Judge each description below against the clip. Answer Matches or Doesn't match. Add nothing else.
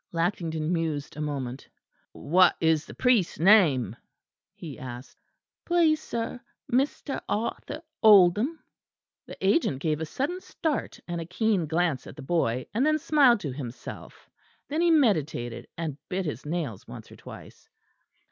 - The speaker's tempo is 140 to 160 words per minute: Matches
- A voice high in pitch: Doesn't match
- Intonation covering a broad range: Matches